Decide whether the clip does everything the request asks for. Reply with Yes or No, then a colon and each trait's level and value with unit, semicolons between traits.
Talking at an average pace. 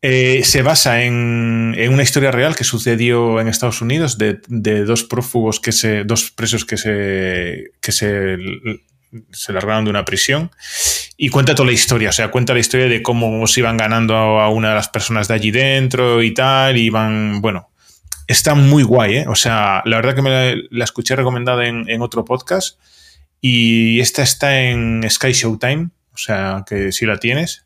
No: fast, 195 wpm